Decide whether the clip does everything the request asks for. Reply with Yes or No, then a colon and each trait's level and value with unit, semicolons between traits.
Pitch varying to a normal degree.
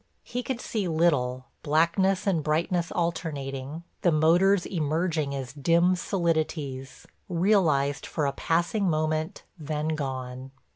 Yes: average, 3.7 semitones